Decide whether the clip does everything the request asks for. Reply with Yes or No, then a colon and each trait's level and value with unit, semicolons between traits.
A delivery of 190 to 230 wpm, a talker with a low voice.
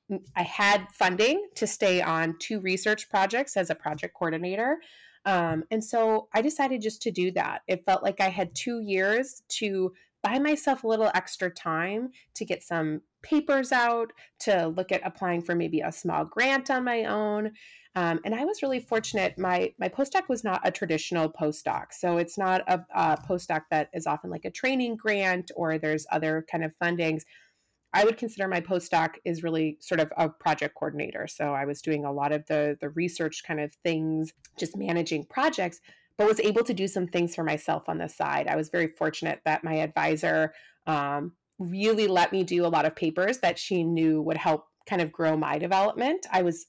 No: average, 200 wpm; medium, 180 Hz